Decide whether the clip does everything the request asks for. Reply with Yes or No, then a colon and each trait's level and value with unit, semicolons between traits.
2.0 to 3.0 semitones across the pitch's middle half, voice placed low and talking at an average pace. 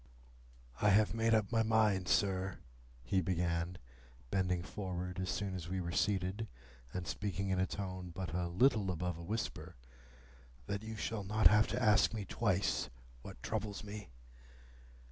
Yes: average, 2.7 semitones; very low, 95 Hz; average, 160 wpm